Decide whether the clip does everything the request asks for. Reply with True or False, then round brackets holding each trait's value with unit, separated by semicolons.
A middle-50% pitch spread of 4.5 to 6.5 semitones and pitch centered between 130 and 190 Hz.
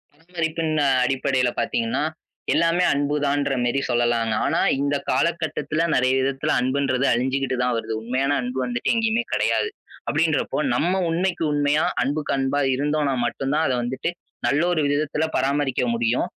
False (3.3 semitones; 140 Hz)